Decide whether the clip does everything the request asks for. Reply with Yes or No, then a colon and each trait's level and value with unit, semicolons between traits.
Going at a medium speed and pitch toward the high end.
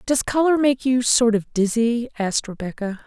Yes: average, 175 wpm; high, 235 Hz